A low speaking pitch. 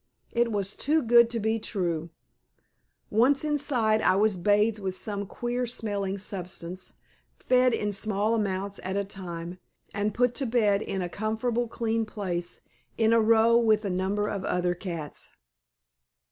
No: high, 210 Hz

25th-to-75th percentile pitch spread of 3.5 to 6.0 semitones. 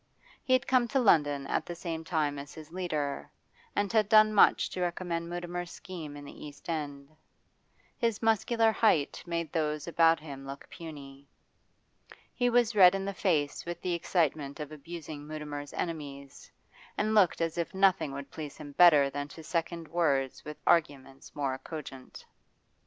Yes: average, 3.9 semitones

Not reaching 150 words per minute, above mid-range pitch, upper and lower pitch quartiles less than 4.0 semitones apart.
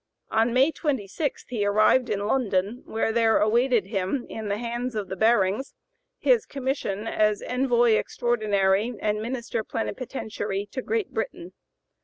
Yes: average, 140 wpm; high, 225 Hz; average, 3.4 semitones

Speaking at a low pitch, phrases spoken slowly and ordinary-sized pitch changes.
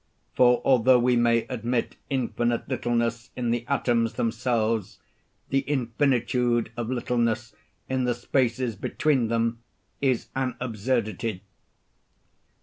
No: low, 120 Hz; slow, 110 wpm; narrow, 1.5 semitones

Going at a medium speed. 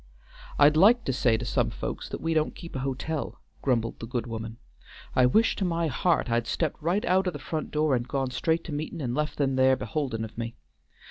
No: fast, 220 wpm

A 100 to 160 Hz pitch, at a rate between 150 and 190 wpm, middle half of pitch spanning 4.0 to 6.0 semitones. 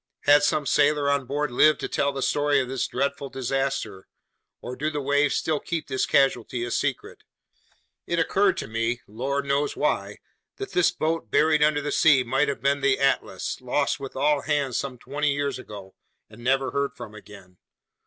No: medium, 140 Hz; average, 185 wpm; narrow, 2.5 semitones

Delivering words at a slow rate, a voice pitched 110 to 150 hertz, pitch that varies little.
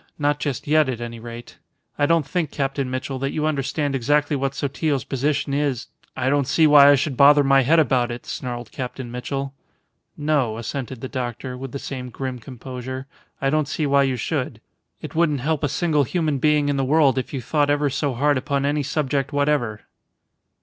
No: average, 200 wpm; medium, 140 Hz; narrow, 2.3 semitones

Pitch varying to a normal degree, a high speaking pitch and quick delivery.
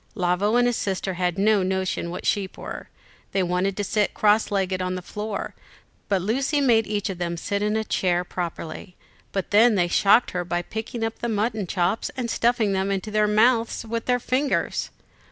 No: average, 3.4 semitones; high, 205 Hz; average, 195 wpm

